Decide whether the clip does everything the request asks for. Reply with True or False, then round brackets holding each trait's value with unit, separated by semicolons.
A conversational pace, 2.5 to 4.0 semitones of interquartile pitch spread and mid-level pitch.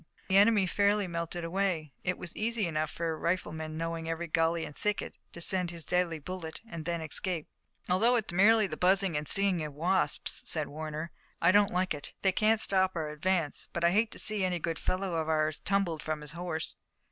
False (210 wpm; 3.2 semitones; 170 Hz)